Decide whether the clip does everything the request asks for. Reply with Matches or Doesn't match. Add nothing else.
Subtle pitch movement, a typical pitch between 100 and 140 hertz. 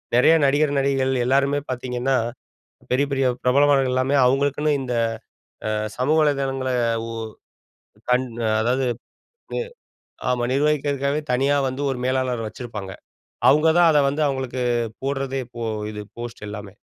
Matches